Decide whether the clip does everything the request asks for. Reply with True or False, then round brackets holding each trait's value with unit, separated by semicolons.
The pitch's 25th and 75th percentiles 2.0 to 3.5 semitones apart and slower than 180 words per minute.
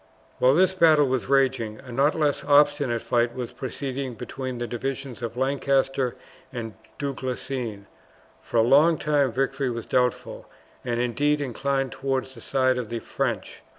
True (2.5 semitones; 155 wpm)